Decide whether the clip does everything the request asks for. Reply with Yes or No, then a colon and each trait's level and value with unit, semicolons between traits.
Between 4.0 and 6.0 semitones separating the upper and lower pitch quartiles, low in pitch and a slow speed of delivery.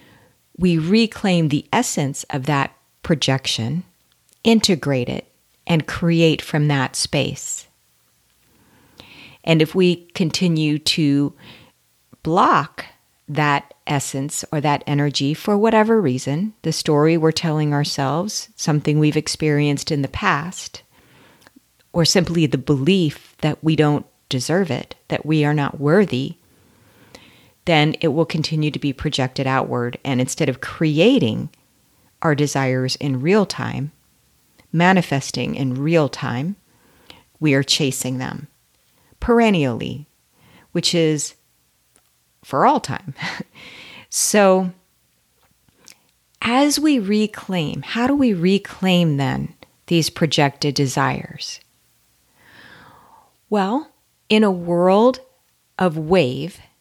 No: average, 4.6 semitones; medium, 155 Hz; slow, 110 wpm